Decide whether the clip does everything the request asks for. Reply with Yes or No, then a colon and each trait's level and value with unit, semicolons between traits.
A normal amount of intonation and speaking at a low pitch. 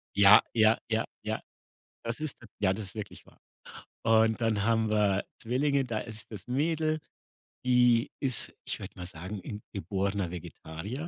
Yes: average, 3.3 semitones; low, 110 Hz